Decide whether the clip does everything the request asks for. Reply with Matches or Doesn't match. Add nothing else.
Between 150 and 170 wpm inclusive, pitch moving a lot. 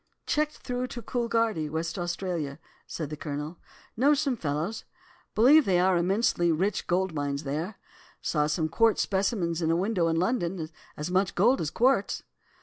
Matches